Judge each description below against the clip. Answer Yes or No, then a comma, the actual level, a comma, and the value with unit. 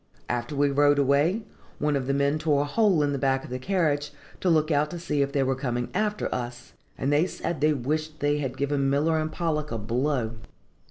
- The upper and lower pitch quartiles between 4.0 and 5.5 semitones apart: No, narrow, 2.4 semitones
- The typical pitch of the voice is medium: Yes, medium, 145 Hz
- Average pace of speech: No, fast, 225 wpm